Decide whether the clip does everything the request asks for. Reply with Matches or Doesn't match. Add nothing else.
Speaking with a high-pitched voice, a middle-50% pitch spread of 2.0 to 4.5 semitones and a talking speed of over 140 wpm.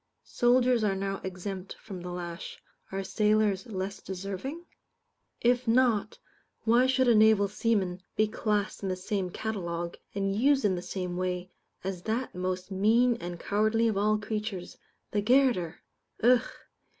Matches